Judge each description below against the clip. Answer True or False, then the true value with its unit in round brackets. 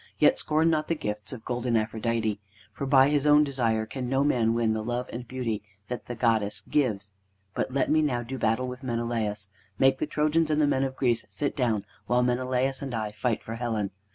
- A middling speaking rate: False (210 wpm)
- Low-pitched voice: True (125 Hz)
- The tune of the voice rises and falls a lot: False (3.2 semitones)